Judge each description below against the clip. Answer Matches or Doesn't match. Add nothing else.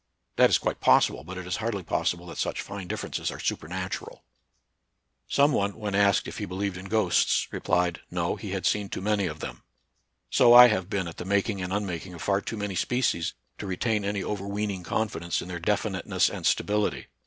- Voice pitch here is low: Matches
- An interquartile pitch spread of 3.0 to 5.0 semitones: Doesn't match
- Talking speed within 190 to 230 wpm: Matches